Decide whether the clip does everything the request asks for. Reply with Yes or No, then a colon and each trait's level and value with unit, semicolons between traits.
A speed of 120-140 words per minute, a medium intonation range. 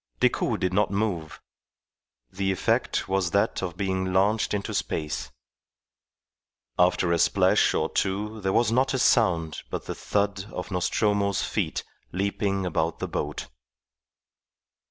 No: slow, 135 wpm; narrow, 2.2 semitones